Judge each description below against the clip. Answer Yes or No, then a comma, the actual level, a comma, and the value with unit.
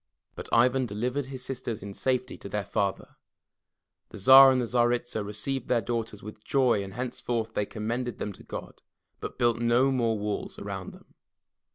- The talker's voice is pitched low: Yes, low, 120 Hz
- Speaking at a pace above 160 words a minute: Yes, average, 170 wpm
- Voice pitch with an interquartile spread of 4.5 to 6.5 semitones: No, average, 3.2 semitones